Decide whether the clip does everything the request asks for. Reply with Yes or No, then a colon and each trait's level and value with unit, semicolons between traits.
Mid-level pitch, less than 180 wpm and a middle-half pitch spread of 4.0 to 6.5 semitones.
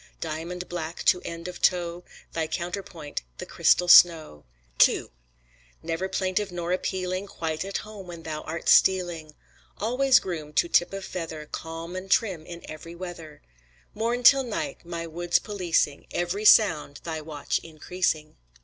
No: medium, 175 Hz; average, 150 wpm; narrow, 2.6 semitones